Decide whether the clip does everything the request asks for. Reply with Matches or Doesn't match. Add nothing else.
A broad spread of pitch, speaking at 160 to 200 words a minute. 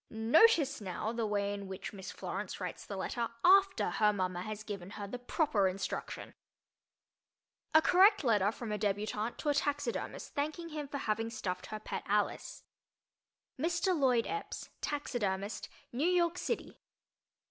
Doesn't match